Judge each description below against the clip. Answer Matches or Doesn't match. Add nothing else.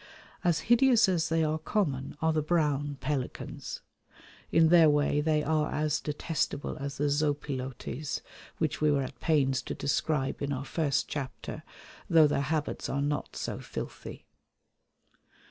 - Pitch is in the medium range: Matches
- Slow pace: Doesn't match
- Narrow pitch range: Matches